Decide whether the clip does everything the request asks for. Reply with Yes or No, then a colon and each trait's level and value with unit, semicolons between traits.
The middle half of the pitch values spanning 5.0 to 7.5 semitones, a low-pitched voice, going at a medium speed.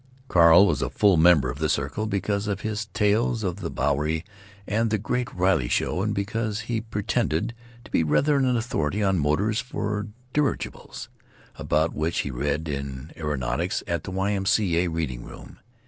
Yes: wide, 5.6 semitones; very low, 95 Hz; average, 175 wpm